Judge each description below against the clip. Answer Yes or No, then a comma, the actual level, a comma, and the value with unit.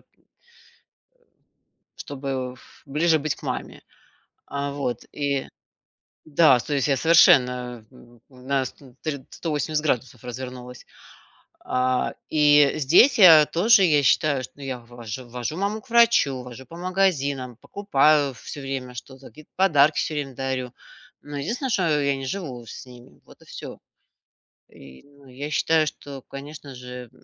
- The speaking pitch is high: No, medium, 140 Hz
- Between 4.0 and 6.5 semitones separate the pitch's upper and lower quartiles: No, average, 3.3 semitones